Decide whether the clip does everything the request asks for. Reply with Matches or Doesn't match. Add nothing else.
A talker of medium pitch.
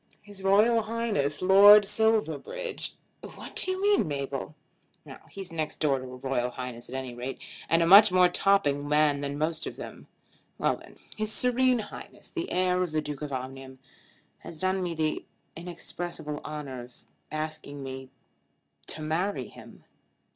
Matches